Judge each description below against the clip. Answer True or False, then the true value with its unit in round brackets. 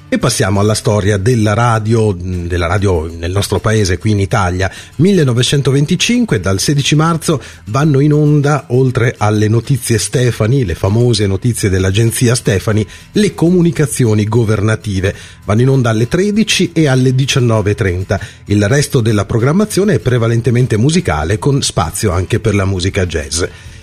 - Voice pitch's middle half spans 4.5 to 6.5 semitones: True (5.1 semitones)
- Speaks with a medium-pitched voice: False (115 Hz)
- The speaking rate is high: False (140 wpm)